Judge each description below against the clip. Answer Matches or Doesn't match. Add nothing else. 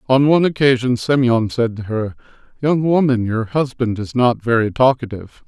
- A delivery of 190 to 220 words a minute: Doesn't match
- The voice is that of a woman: Doesn't match